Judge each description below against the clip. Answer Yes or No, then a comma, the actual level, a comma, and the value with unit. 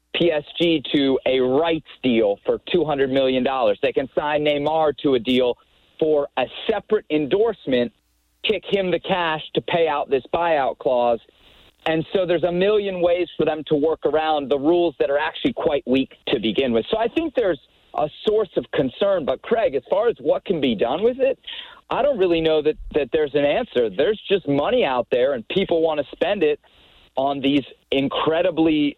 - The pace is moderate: Yes, average, 190 wpm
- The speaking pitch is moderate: Yes, medium, 160 Hz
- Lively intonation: Yes, wide, 6.2 semitones